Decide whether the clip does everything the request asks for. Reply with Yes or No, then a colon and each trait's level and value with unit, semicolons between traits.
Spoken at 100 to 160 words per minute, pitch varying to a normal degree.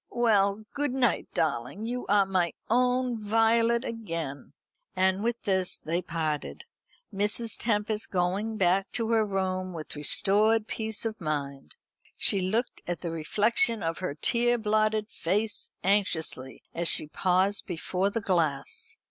Yes: average, 140 wpm; average, 4.4 semitones